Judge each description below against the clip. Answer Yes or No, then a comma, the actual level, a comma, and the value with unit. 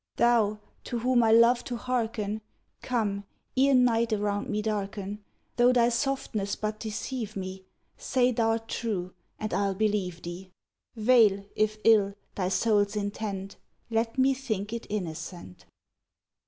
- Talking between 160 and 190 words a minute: No, slow, 135 wpm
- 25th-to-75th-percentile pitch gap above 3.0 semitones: No, average, 2.7 semitones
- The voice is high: Yes, high, 215 Hz